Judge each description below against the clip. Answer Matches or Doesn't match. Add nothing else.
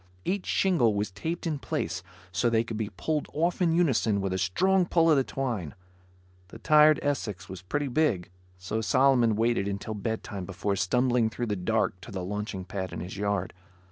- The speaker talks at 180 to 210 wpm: Matches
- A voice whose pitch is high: Doesn't match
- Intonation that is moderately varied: Doesn't match